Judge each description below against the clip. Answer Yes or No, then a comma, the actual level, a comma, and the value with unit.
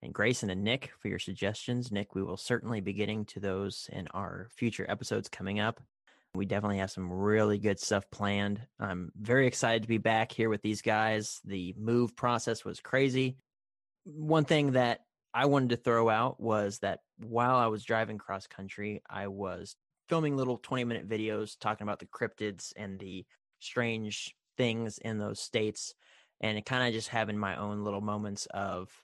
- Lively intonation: No, average, 3.0 semitones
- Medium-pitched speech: No, low, 110 Hz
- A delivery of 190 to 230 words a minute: No, average, 180 wpm